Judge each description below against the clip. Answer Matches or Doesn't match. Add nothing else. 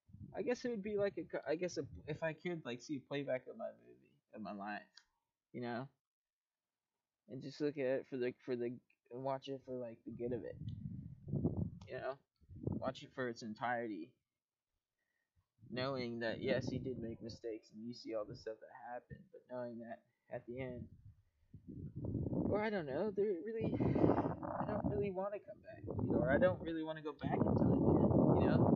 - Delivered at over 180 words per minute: Matches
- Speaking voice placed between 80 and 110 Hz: Doesn't match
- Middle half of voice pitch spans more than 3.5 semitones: Matches